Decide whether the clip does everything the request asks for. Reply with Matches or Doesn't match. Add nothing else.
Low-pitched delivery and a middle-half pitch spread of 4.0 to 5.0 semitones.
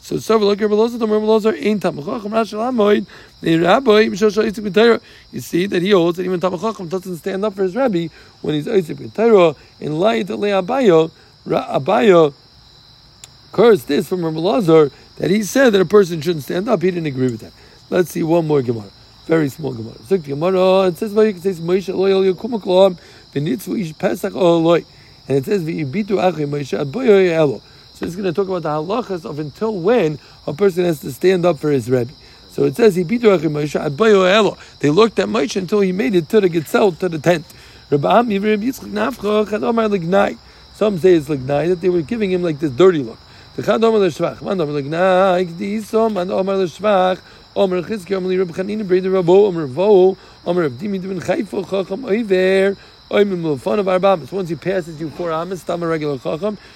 Doesn't match